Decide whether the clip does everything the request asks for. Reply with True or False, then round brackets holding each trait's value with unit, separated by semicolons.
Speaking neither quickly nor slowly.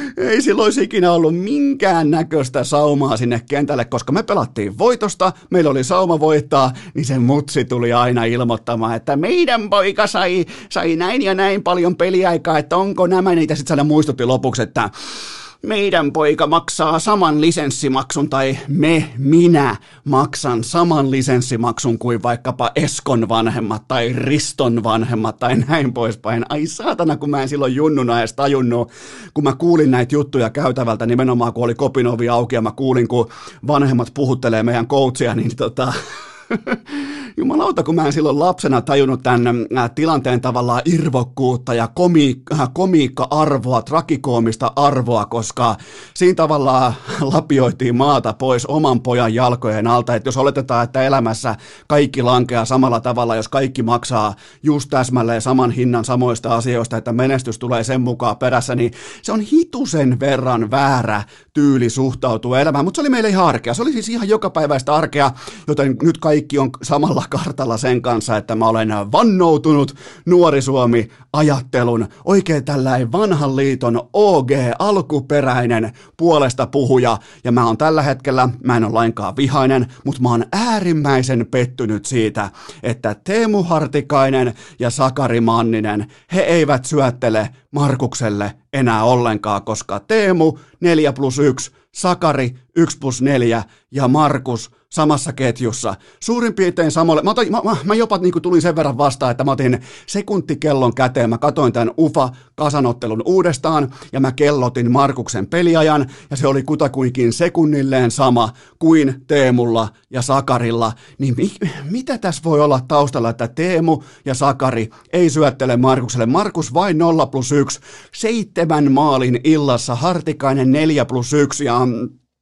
True (145 wpm)